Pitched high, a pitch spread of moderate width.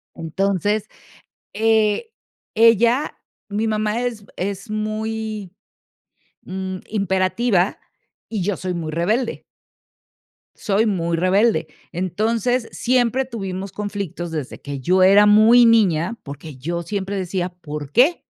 Yes: high, 200 Hz; average, 3.6 semitones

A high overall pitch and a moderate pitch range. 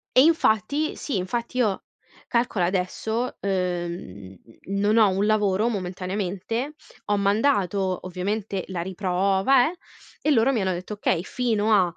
Yes: high, 200 Hz; average, 3.6 semitones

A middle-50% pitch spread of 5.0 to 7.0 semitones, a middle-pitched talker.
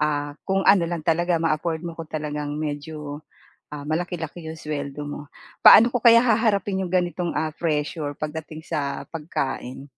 No: average, 2.9 semitones; medium, 160 Hz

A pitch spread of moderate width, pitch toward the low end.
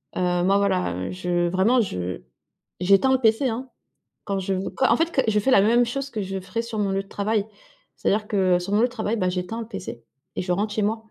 No: average, 3.8 semitones; high, 200 Hz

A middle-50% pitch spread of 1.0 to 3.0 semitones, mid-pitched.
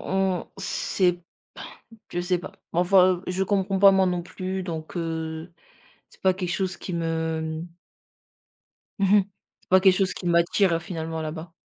Yes: narrow, 2.4 semitones; medium, 180 Hz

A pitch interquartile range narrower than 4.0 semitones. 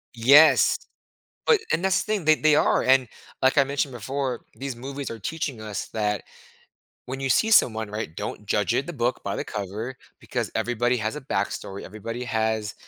No: average, 4.3 semitones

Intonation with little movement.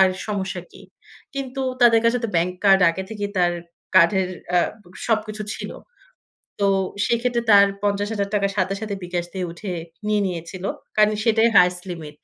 No: average, 3.1 semitones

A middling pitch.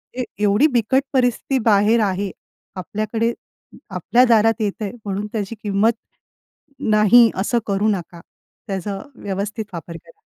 No: high, 210 Hz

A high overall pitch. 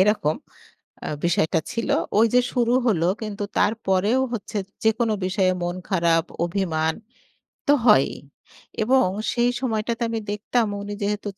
Yes: high, 210 Hz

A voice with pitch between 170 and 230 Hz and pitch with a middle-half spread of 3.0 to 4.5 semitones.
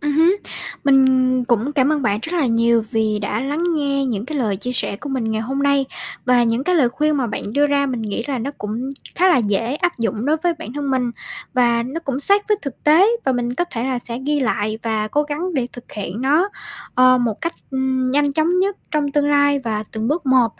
No: very high, 265 Hz; average, 4.0 semitones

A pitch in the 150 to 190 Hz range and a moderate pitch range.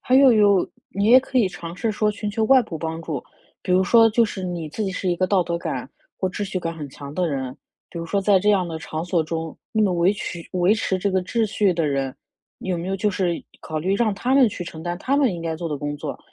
Yes: medium, 185 Hz; average, 3.9 semitones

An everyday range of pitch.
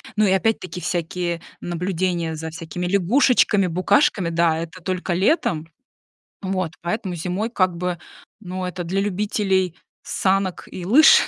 No: narrow, 2.2 semitones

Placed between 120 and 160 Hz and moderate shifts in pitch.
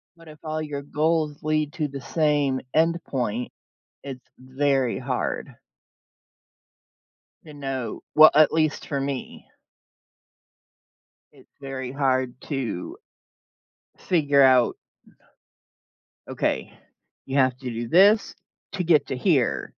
Yes: medium, 140 Hz; average, 3.0 semitones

